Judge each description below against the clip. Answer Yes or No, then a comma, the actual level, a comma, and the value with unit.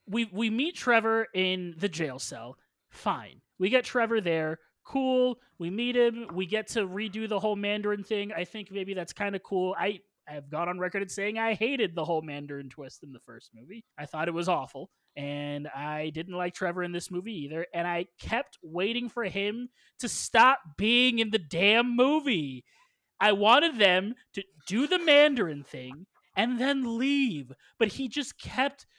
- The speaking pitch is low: No, high, 200 Hz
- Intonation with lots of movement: Yes, wide, 5.8 semitones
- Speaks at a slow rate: No, average, 190 wpm